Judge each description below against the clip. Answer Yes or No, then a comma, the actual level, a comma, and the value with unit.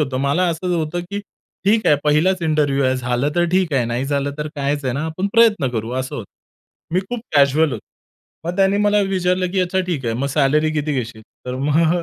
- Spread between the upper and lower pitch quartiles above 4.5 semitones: Yes, average, 5.1 semitones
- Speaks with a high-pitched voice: No, medium, 150 Hz